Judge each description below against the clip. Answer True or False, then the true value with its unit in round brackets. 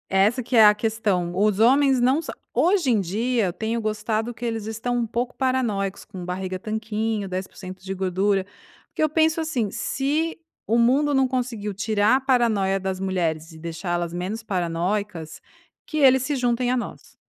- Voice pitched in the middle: False (220 Hz)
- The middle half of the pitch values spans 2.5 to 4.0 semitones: False (4.7 semitones)